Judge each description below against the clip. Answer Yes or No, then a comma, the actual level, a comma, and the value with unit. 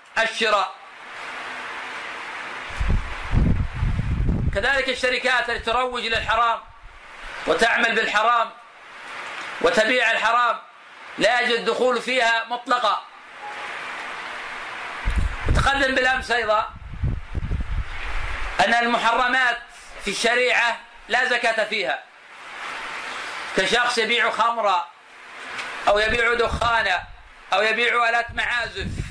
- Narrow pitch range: Yes, narrow, 2.0 semitones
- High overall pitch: Yes, high, 230 Hz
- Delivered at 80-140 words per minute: No, average, 70 wpm